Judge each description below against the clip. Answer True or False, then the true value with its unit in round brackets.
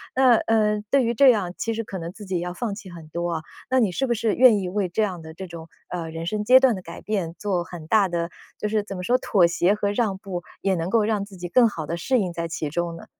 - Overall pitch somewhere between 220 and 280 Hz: False (195 Hz)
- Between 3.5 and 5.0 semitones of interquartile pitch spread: True (4.2 semitones)